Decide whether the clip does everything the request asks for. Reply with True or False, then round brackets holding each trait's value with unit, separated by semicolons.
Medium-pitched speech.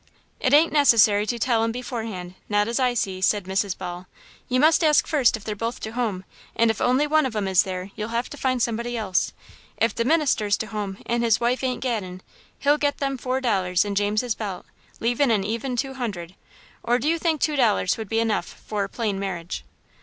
False (230 Hz)